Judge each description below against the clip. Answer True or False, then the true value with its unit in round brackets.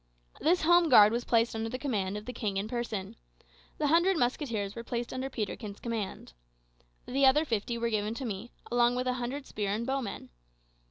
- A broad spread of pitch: False (3.7 semitones)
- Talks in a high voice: True (235 Hz)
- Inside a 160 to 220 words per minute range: True (195 wpm)